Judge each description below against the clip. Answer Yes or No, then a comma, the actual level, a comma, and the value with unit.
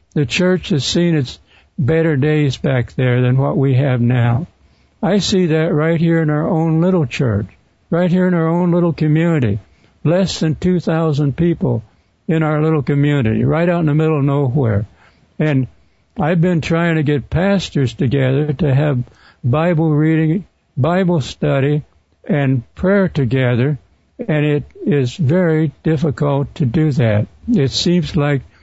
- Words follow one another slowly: No, average, 155 wpm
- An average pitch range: Yes, average, 3.9 semitones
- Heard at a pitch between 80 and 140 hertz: No, medium, 150 Hz